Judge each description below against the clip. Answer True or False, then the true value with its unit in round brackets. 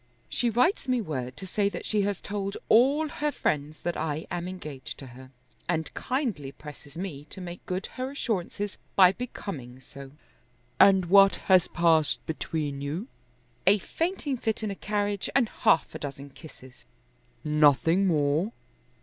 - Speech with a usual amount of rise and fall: False (5.9 semitones)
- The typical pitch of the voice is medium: True (180 Hz)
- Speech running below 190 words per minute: True (160 wpm)